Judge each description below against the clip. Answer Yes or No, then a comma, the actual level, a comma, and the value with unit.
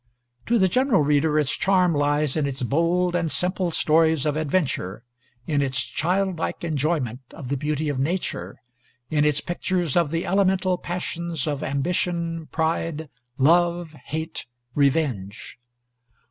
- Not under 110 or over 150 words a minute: Yes, slow, 135 wpm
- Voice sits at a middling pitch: Yes, medium, 160 Hz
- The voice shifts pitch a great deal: No, average, 3.3 semitones